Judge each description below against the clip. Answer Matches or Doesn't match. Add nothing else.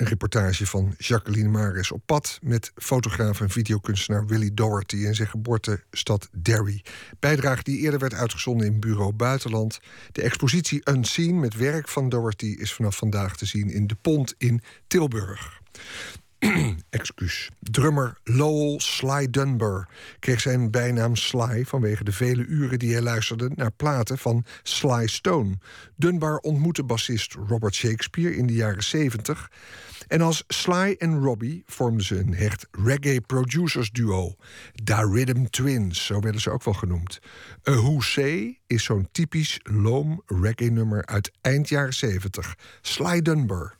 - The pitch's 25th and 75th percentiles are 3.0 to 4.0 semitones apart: Doesn't match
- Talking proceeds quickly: Doesn't match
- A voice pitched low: Matches